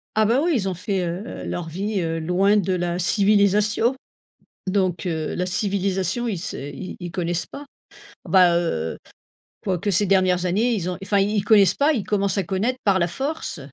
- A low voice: No, high, 190 Hz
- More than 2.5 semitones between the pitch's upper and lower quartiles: Yes, average, 2.9 semitones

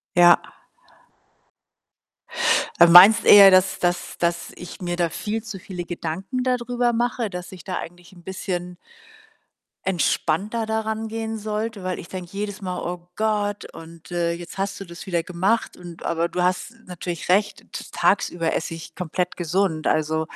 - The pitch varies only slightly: No, average, 3.2 semitones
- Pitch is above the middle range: No, medium, 180 Hz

